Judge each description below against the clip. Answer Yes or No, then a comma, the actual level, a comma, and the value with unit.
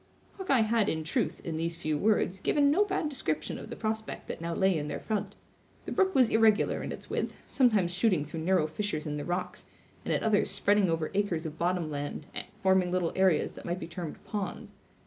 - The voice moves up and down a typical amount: Yes, average, 5.0 semitones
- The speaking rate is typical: No, fast, 210 wpm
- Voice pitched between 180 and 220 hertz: Yes, medium, 185 Hz